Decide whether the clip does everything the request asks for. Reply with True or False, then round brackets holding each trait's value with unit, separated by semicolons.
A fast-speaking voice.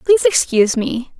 False (150 wpm)